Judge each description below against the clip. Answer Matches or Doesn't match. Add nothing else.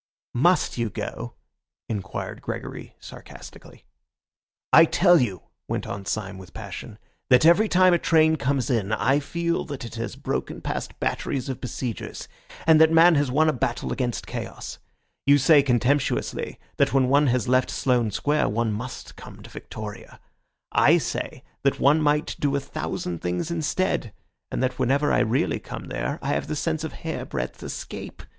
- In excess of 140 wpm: Matches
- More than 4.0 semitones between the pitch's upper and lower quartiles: Matches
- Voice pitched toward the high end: Doesn't match